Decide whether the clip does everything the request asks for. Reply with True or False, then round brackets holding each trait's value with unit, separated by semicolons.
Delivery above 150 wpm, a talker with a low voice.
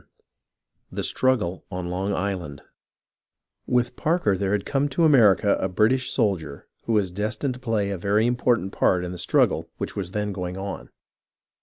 True (175 wpm; 100 Hz)